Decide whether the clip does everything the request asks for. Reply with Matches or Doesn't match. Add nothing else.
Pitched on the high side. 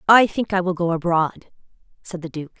Doesn't match